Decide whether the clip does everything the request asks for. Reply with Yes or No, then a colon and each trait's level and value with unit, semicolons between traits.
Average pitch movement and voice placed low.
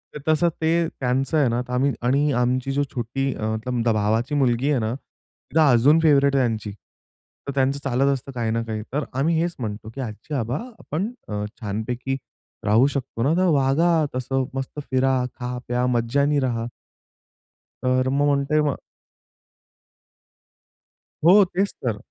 Yes: average, 3.2 semitones; low, 130 Hz